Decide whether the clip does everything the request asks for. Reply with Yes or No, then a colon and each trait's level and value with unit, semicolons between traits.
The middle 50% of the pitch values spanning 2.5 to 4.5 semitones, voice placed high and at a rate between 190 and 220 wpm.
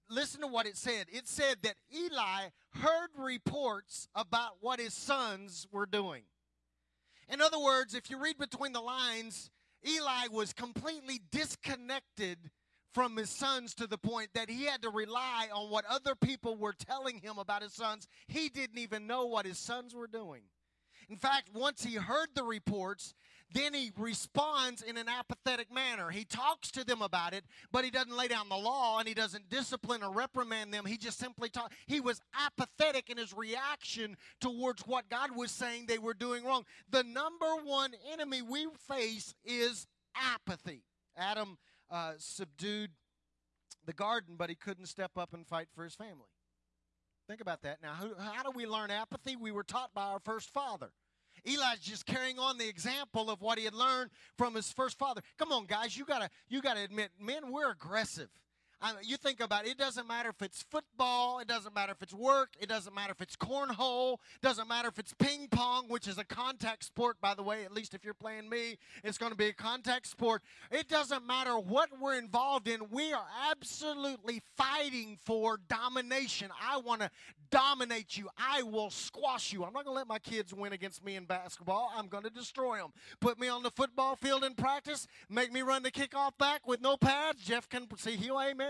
Yes: average, 4.1 semitones; high, 235 Hz; average, 195 wpm